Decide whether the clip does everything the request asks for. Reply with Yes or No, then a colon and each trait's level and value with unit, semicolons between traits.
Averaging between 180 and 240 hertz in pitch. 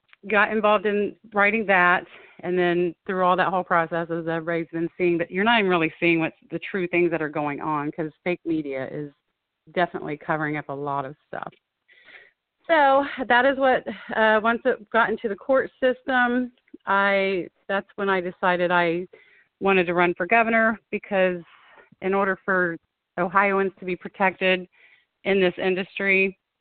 Yes: medium, 185 Hz